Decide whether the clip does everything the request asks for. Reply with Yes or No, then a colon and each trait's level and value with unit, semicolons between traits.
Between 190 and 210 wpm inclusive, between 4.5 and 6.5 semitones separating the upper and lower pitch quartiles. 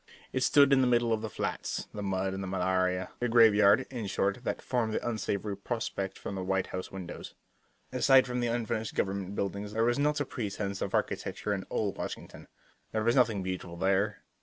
No: average, 200 wpm; average, 3.7 semitones